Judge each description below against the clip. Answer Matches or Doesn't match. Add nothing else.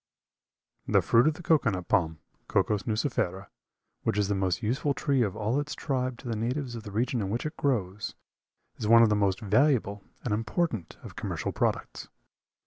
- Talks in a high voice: Doesn't match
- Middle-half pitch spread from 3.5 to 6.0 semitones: Matches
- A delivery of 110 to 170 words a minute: Doesn't match